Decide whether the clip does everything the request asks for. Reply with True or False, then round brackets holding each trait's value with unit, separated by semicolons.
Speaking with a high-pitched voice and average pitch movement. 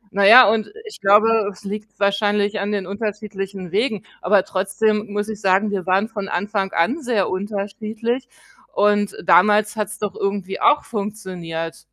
False (205 Hz; 1.7 semitones)